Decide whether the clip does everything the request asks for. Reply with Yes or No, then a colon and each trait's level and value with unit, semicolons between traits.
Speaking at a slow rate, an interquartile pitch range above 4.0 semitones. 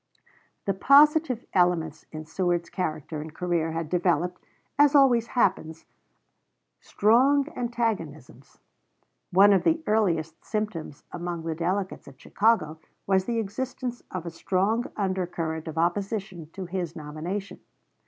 Yes: slow, 125 wpm; average, 5.3 semitones